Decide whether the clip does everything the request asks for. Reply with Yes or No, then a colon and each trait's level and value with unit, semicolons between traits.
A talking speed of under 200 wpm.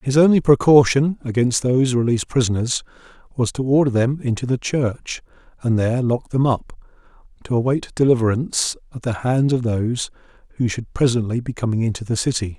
Yes: average, 165 wpm